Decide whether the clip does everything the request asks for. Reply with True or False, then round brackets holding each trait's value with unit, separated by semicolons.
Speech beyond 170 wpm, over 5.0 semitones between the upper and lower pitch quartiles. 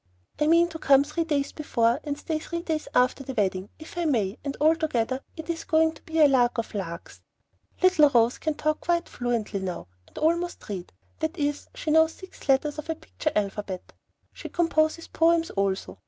True (195 wpm; 5.5 semitones)